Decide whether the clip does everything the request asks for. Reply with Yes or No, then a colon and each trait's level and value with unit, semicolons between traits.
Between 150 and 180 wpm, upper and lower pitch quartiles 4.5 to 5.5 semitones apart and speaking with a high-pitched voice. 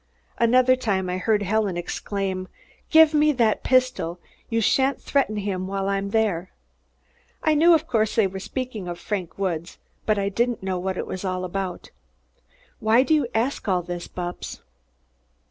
Yes: average, 170 wpm; average, 5.1 semitones; high, 200 Hz